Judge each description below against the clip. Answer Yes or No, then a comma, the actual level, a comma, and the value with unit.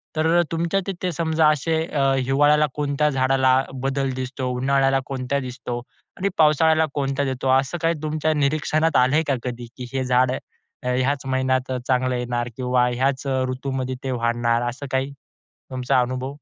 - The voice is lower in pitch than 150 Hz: Yes, low, 135 Hz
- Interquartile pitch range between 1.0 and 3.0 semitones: Yes, average, 2.7 semitones